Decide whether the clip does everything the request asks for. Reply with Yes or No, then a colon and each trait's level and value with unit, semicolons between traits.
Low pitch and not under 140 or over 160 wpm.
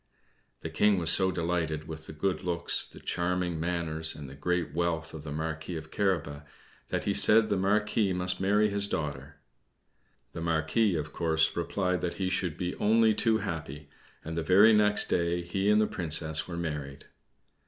No: very low, 85 Hz; average, 180 wpm